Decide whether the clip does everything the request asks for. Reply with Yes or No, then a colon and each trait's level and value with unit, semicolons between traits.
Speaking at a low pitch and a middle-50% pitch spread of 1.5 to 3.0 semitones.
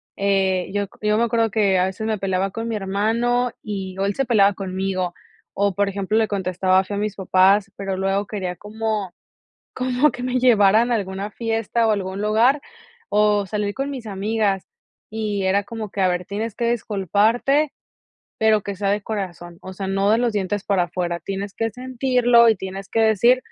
No: high, 205 Hz; average, 2.7 semitones